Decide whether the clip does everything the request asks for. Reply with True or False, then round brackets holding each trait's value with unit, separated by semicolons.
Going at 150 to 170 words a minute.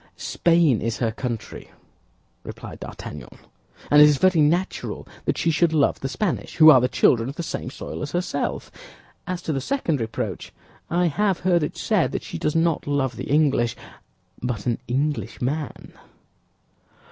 True (165 wpm)